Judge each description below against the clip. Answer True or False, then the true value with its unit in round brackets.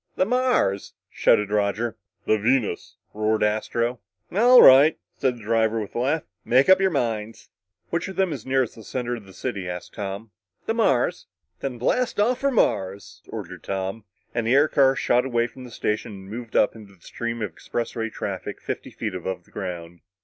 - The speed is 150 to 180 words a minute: False (190 wpm)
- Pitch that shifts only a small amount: False (4.4 semitones)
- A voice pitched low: True (115 Hz)